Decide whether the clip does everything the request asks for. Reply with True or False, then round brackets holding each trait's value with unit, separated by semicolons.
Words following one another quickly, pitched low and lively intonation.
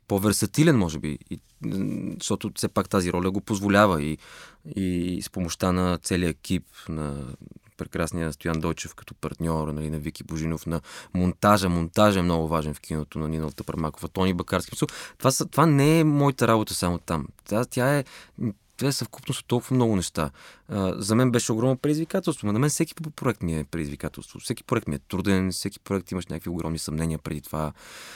True (185 wpm; 95 Hz; 5.9 semitones)